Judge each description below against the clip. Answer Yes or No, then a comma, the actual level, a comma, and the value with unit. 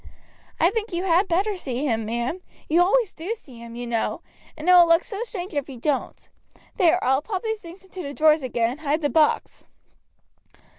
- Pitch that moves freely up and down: Yes, wide, 5.9 semitones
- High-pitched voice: Yes, very high, 325 Hz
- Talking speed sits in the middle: No, fast, 210 wpm